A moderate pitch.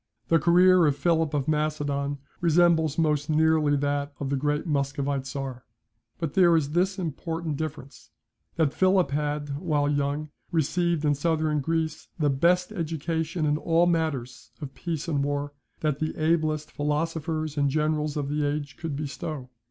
Yes: medium, 150 Hz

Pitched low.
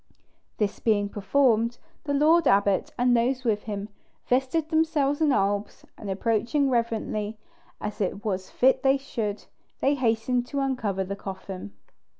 No: high, 230 Hz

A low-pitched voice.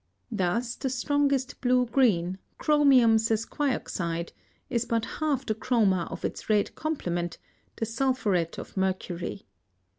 No: high, 225 Hz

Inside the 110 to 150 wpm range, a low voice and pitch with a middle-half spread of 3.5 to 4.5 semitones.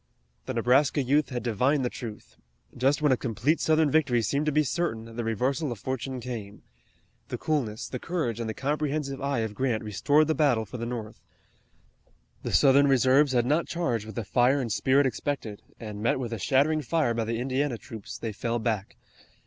No: average, 195 wpm; low, 130 Hz; average, 3.9 semitones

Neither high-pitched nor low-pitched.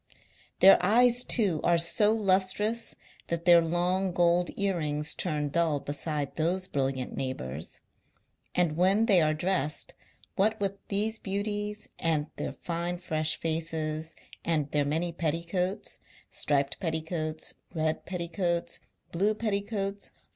Yes: medium, 170 Hz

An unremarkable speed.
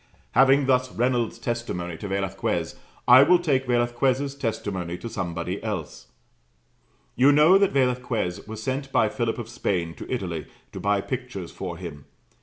Yes: average, 150 wpm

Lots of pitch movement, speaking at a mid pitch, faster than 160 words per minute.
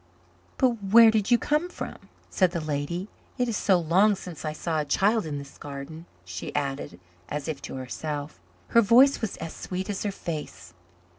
Yes: wide, 6.3 semitones; medium, 170 Hz; average, 190 wpm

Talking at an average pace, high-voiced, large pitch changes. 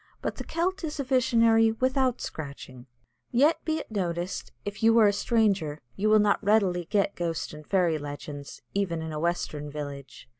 Yes: average, 180 wpm; high, 200 Hz; wide, 6.6 semitones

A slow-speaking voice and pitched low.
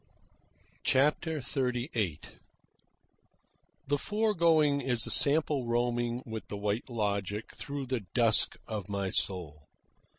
Yes: slow, 110 wpm; low, 120 Hz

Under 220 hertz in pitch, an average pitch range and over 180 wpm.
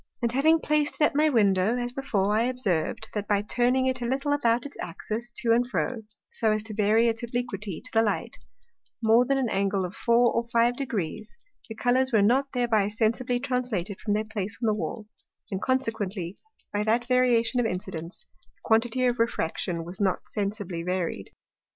No: high, 225 Hz; average, 3.4 semitones; average, 190 wpm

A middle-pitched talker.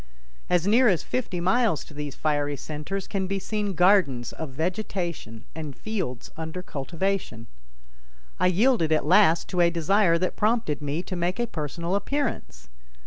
Yes: medium, 175 Hz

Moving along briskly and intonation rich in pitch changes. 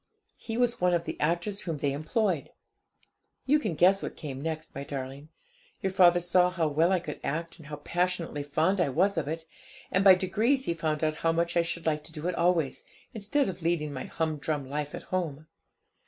No: fast, 210 wpm; average, 3.3 semitones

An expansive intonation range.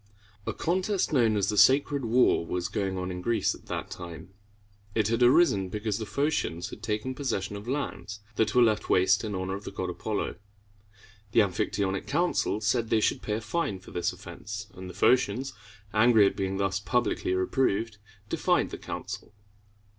No: average, 4.0 semitones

